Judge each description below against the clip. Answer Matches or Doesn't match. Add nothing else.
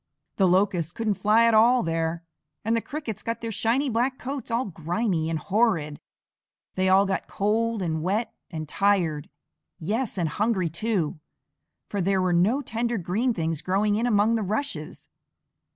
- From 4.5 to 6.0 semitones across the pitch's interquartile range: Matches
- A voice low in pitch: Doesn't match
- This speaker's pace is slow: Doesn't match